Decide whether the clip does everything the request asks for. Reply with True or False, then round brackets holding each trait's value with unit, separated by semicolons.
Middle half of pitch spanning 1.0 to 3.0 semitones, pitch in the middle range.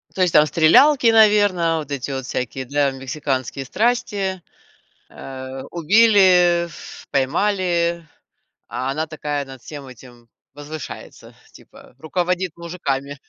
False (5.2 semitones; 155 Hz)